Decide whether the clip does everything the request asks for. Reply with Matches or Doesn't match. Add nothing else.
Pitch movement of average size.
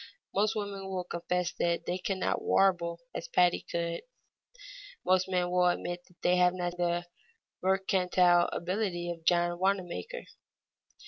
Doesn't match